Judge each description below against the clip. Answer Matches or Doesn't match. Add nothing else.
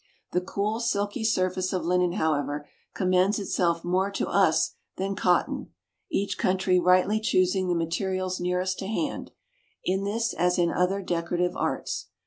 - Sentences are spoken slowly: Doesn't match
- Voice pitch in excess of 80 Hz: Matches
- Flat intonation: Matches